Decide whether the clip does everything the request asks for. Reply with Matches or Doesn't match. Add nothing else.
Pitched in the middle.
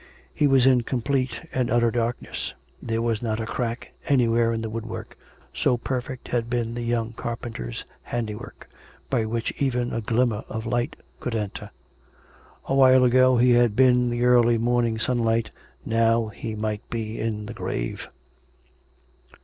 Doesn't match